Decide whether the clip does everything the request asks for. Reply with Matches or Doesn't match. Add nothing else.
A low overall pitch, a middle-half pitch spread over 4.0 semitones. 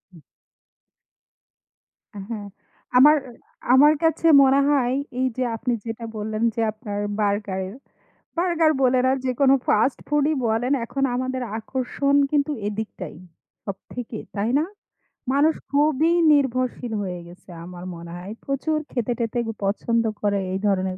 Doesn't match